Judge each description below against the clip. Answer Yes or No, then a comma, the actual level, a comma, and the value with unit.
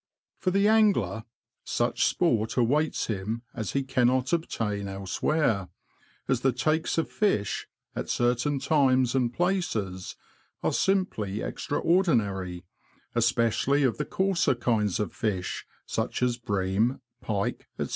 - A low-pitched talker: Yes, low, 120 Hz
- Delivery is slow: Yes, slow, 125 wpm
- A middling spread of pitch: No, wide, 6.3 semitones